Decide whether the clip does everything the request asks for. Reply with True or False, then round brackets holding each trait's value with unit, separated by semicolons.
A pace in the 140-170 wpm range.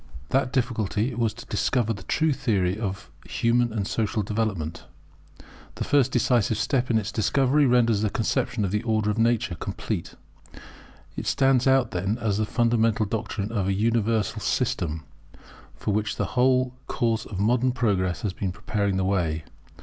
True (165 wpm)